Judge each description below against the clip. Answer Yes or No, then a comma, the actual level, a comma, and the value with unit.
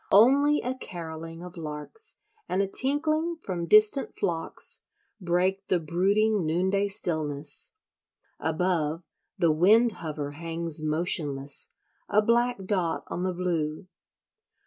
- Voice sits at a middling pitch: Yes, medium, 180 Hz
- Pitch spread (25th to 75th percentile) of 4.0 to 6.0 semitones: Yes, average, 4.8 semitones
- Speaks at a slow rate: Yes, slow, 115 wpm